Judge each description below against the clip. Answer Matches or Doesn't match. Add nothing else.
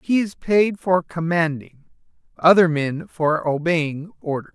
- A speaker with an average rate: Doesn't match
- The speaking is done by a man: Matches